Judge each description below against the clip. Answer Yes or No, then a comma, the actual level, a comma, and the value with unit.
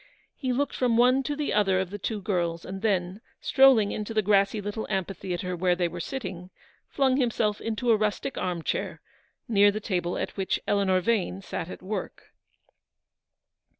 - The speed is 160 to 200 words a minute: Yes, average, 175 wpm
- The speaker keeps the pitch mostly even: No, average, 3.6 semitones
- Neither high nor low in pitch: No, high, 205 Hz